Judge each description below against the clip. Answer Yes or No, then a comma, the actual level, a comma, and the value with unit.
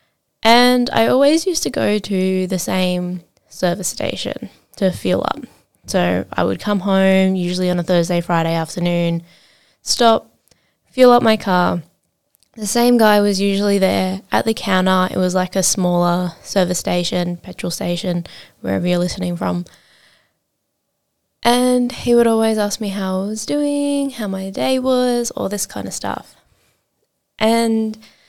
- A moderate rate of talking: Yes, average, 155 wpm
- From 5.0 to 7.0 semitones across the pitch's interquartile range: No, average, 3.9 semitones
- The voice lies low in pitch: No, high, 190 Hz